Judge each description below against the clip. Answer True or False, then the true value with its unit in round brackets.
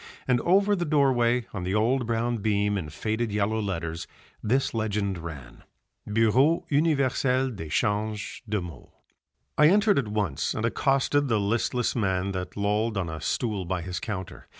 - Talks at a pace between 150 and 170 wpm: True (155 wpm)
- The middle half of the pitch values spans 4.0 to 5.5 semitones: True (4.7 semitones)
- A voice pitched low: True (110 Hz)